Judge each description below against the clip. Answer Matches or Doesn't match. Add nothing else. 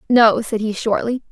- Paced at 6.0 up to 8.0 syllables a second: Doesn't match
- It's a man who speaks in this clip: Doesn't match